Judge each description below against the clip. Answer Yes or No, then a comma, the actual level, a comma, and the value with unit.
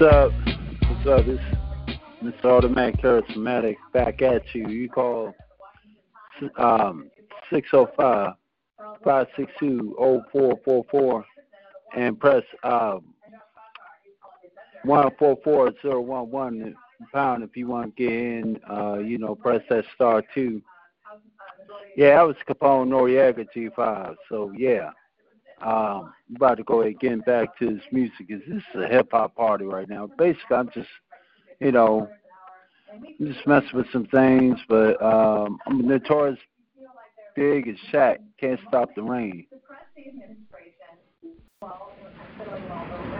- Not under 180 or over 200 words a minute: No, slow, 135 wpm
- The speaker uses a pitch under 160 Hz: Yes, low, 135 Hz